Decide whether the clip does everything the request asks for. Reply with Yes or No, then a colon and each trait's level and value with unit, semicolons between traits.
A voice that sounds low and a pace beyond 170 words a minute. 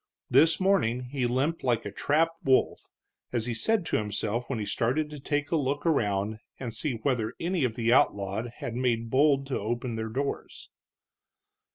Yes: low, 125 Hz; average, 180 wpm